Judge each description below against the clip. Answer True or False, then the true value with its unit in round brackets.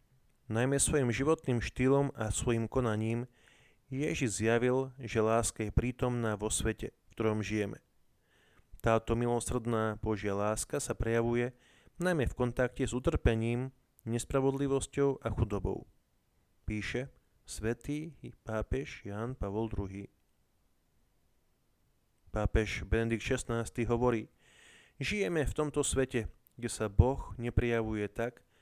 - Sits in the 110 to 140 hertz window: True (115 Hz)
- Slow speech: True (105 wpm)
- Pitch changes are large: False (3.0 semitones)